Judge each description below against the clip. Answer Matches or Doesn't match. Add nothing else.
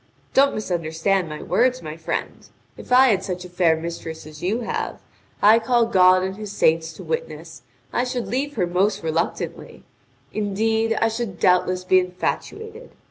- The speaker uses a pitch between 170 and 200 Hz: Matches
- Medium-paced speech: Matches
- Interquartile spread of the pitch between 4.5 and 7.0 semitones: Matches